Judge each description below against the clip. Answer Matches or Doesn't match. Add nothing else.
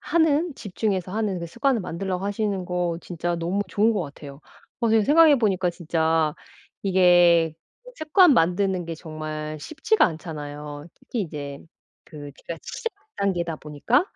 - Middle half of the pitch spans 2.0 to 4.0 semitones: Doesn't match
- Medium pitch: Matches